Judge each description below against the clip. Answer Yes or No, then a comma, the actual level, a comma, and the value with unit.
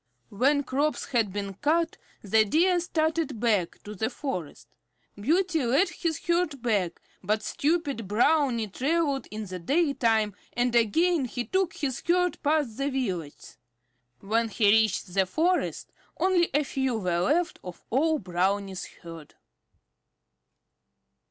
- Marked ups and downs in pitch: Yes, wide, 7.4 semitones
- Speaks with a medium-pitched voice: No, high, 245 Hz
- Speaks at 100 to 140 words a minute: Yes, slow, 135 wpm